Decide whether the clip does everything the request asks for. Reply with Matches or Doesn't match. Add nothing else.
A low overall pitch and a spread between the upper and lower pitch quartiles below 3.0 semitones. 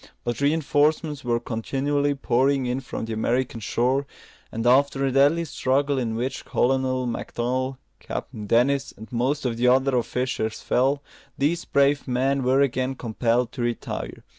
Matches